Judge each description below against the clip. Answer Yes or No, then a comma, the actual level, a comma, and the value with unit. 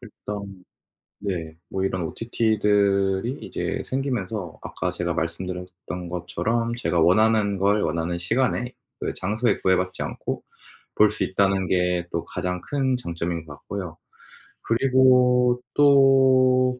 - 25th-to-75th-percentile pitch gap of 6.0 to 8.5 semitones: No, wide, 5.4 semitones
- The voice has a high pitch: No, low, 100 Hz